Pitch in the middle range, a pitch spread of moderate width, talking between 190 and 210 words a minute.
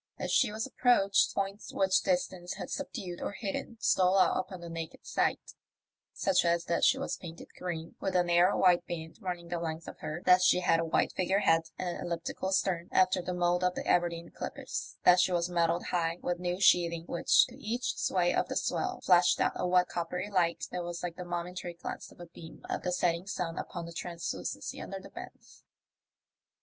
No: medium, 175 Hz; narrow, 1.4 semitones; fast, 205 wpm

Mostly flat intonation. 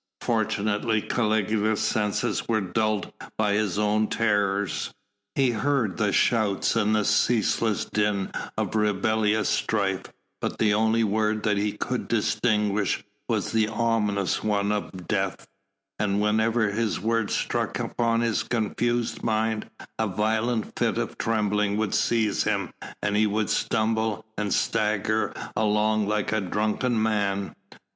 Yes: narrow, 1.3 semitones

